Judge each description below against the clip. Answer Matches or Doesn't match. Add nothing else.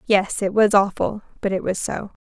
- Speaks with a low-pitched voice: Doesn't match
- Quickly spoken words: Matches